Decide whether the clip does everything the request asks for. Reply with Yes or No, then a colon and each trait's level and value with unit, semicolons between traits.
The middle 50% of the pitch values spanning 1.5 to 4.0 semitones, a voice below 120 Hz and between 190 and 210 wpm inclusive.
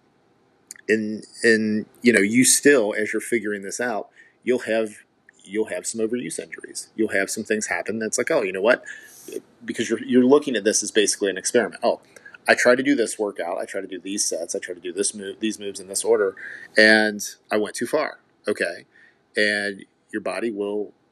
Yes: average, 3.2 semitones; low, 110 Hz; fast, 205 wpm